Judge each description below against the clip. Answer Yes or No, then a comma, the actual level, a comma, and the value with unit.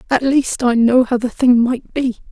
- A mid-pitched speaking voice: No, very high, 250 Hz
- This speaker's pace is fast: Yes, fast, 235 wpm